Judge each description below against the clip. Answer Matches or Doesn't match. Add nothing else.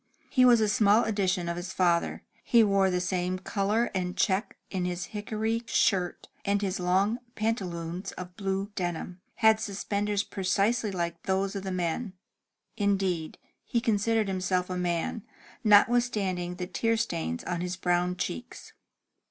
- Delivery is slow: Doesn't match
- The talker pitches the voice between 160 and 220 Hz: Matches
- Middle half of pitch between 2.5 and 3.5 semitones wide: Matches